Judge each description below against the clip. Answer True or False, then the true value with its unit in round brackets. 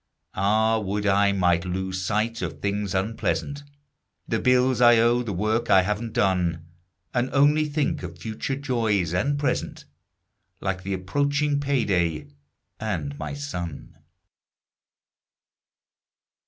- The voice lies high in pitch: False (105 Hz)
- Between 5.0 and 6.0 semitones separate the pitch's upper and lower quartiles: True (5.3 semitones)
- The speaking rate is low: True (120 wpm)